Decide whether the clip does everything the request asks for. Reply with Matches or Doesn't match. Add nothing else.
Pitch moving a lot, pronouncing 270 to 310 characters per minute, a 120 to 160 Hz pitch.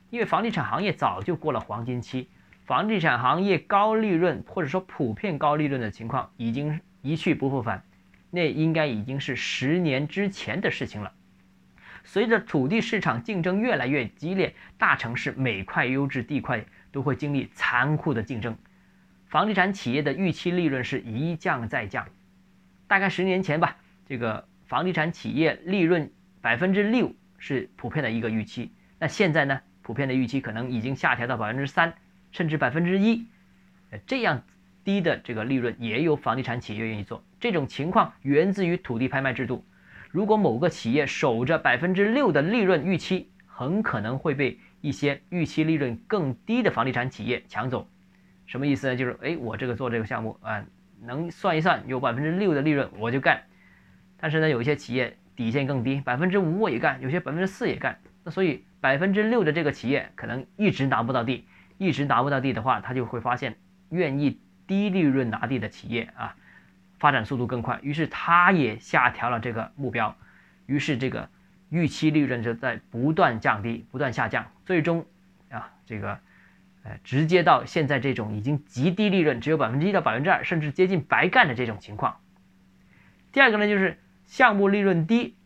Matches